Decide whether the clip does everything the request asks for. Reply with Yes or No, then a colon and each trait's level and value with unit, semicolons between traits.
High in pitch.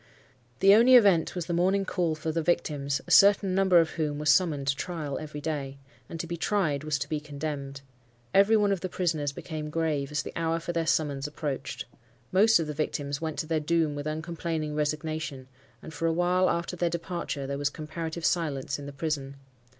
No: medium, 160 Hz